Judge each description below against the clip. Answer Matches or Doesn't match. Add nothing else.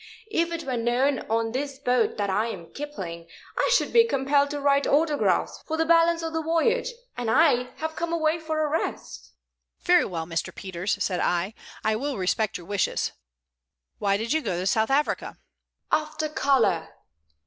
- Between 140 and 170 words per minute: Doesn't match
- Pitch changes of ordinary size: Doesn't match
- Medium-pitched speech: Doesn't match